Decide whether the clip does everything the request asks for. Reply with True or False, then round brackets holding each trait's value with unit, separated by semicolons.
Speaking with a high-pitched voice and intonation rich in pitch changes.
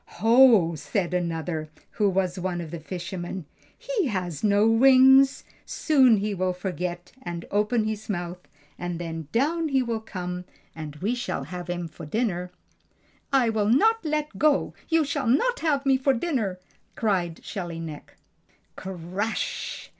True (200 Hz; 6.6 semitones)